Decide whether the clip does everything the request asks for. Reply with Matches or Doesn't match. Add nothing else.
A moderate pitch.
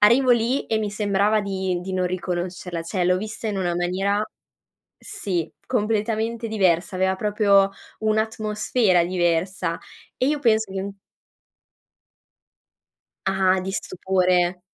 Doesn't match